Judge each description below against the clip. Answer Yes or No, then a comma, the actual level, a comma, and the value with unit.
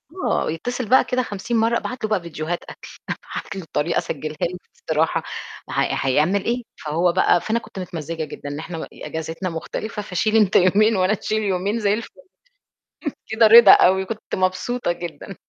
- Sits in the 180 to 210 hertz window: Yes, high, 190 Hz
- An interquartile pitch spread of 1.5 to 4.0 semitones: No, average, 4.8 semitones